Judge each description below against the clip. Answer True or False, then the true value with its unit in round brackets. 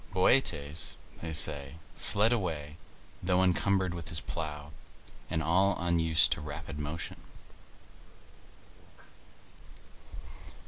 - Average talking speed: False (90 wpm)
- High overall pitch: False (80 Hz)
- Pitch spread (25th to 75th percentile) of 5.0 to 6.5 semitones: False (3.5 semitones)